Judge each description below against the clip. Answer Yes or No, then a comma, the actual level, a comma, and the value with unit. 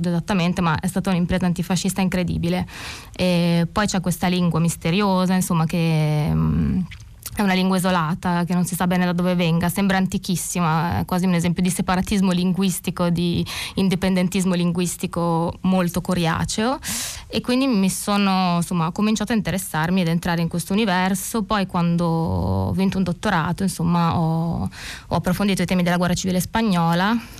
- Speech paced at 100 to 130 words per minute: No, average, 155 wpm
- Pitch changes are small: Yes, narrow, 1.7 semitones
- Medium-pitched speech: Yes, medium, 180 Hz